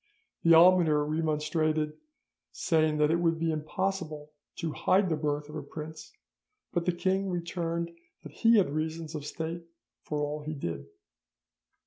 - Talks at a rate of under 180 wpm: Yes, average, 145 wpm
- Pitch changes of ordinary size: No, narrow, 2.0 semitones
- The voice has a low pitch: No, medium, 160 Hz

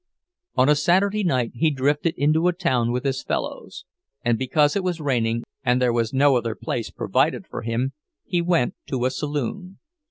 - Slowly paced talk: No, average, 185 wpm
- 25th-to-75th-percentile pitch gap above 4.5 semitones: Yes, average, 5.0 semitones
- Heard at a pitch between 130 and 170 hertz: Yes, low, 135 Hz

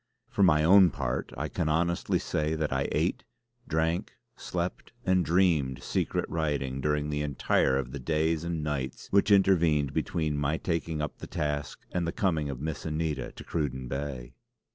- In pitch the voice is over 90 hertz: No, very low, 75 Hz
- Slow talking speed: No, average, 170 wpm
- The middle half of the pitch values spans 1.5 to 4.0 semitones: Yes, average, 2.8 semitones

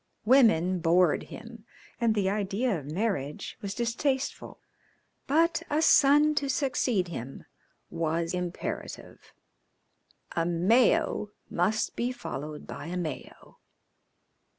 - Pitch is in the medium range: No, high, 205 Hz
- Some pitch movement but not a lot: No, wide, 6.7 semitones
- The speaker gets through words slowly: Yes, slow, 105 wpm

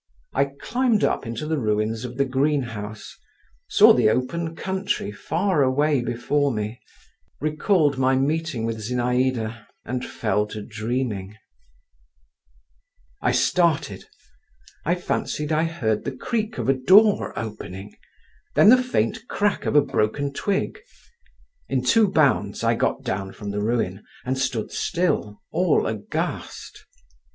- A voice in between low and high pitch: No, low, 130 Hz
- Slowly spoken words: Yes, slow, 130 wpm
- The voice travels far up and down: Yes, wide, 6.7 semitones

